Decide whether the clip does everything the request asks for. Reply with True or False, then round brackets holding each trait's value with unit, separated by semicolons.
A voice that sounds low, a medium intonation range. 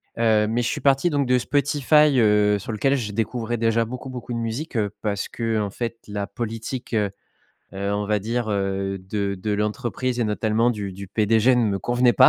True (115 Hz; 3.0 semitones)